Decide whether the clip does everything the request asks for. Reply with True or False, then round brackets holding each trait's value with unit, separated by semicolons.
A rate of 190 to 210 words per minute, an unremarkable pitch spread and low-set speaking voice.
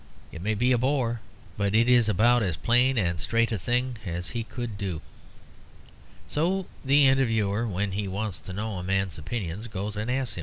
True (195 wpm; 3.9 semitones; 110 Hz)